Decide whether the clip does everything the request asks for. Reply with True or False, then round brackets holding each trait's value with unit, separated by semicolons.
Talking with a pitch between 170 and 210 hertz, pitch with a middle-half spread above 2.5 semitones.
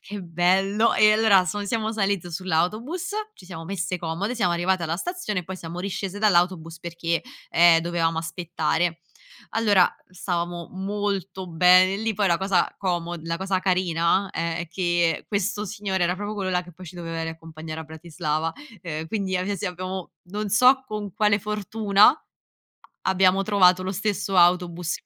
True (185 Hz; 2.9 semitones)